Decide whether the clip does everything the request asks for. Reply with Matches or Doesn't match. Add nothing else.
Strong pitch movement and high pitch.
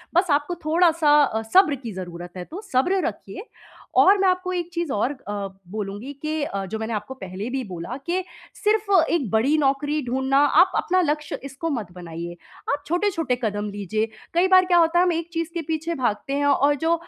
Matches